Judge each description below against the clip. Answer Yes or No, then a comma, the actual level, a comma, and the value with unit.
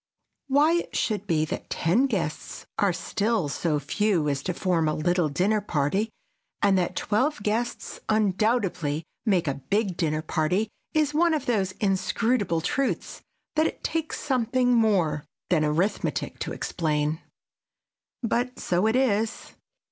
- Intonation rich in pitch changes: Yes, wide, 6.2 semitones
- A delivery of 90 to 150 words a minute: Yes, average, 140 wpm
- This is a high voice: Yes, high, 200 Hz